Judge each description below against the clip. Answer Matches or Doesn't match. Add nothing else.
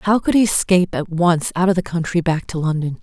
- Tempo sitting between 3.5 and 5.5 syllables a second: Doesn't match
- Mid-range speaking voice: Matches